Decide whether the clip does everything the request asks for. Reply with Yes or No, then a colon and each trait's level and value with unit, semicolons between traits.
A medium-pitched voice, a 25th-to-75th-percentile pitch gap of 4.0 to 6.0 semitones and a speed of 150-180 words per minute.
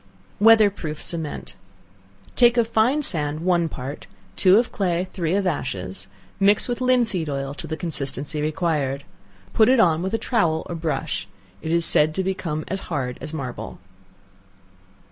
Yes: medium, 170 Hz; average, 5.2 semitones; average, 160 wpm